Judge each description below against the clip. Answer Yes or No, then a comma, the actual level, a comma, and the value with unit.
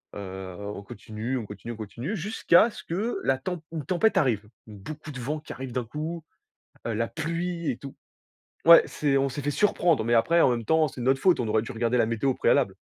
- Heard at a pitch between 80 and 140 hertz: Yes, low, 135 Hz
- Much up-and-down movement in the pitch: Yes, wide, 6.3 semitones